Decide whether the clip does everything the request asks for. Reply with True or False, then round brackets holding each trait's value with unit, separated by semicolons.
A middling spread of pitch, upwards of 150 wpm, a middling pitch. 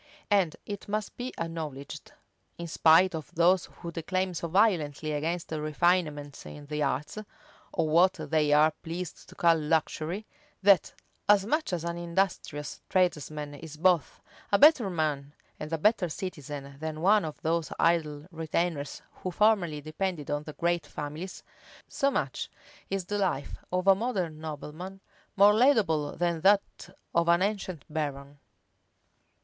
False (3.7 semitones; 145 wpm; 170 Hz)